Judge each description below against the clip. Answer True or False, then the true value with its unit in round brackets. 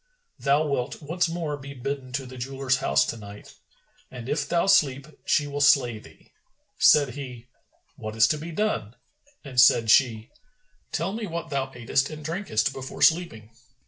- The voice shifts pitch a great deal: False (3.8 semitones)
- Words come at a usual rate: True (170 wpm)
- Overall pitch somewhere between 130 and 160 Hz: True (135 Hz)